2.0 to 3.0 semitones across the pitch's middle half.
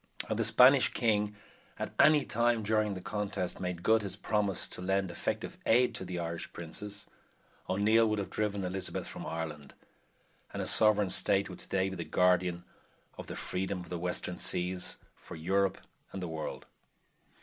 Yes: average, 2.7 semitones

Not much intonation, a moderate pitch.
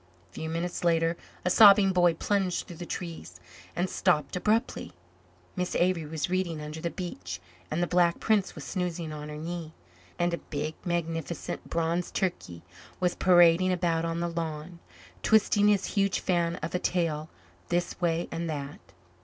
Yes: narrow, 2.1 semitones; medium, 170 Hz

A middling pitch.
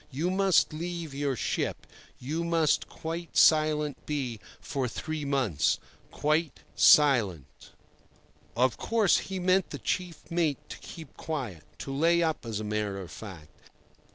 Yes: medium, 150 Hz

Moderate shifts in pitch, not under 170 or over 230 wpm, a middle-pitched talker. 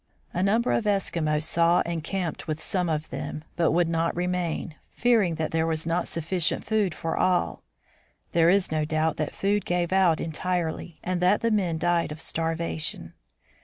No: narrow, 2.3 semitones; average, 175 wpm; medium, 170 Hz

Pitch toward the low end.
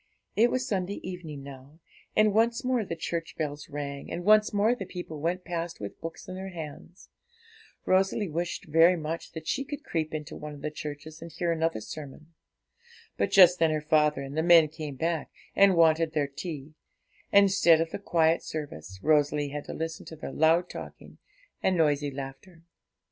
No: medium, 165 Hz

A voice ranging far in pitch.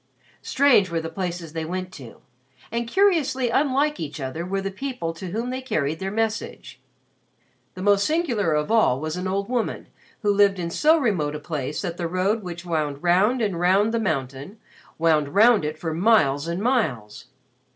Yes: wide, 6.0 semitones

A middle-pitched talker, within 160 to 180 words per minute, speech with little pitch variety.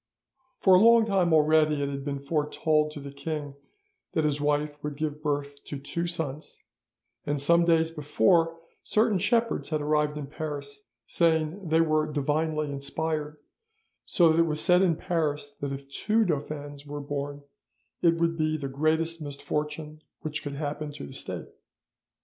Yes: medium, 150 Hz; average, 165 wpm; narrow, 2.1 semitones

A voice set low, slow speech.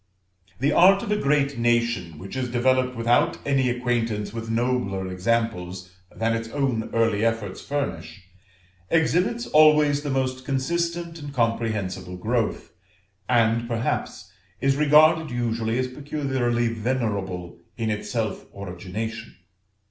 Yes: low, 120 Hz; slow, 125 wpm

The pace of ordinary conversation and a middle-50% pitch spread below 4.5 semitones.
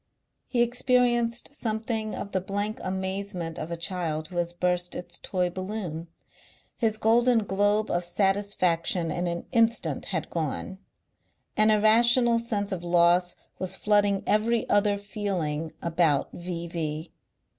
No: slow, 130 wpm; average, 3.9 semitones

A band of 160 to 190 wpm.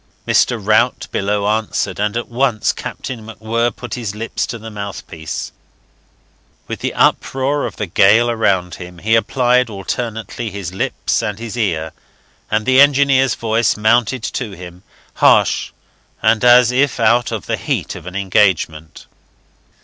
No: average, 150 wpm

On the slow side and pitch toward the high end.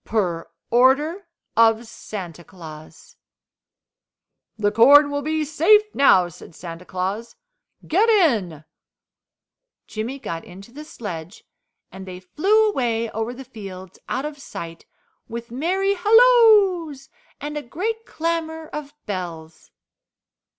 Yes: slow, 115 wpm; high, 245 Hz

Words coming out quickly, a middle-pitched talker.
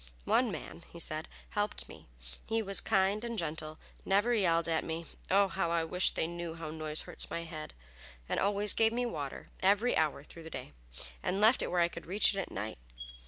Yes: fast, 210 wpm; medium, 170 Hz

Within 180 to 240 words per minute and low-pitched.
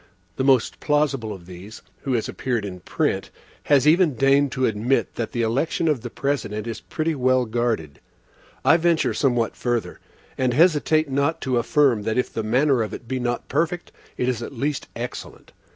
Yes: average, 185 wpm; low, 130 Hz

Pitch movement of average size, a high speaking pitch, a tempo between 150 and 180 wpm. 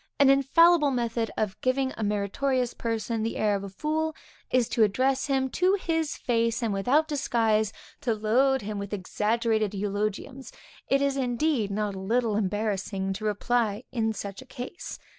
Yes: average, 4.3 semitones; high, 230 Hz; average, 165 wpm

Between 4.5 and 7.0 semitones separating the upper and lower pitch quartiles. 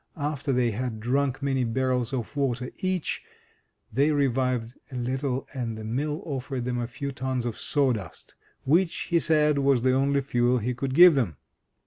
No: narrow, 2.5 semitones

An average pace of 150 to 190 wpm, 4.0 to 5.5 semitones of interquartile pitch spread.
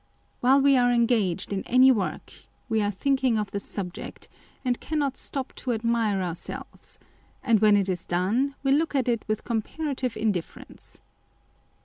Yes: average, 160 wpm; average, 4.4 semitones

